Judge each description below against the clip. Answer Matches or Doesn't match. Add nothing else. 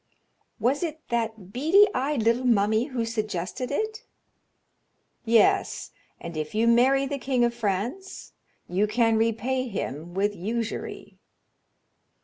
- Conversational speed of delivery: Doesn't match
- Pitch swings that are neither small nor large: Matches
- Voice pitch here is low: Doesn't match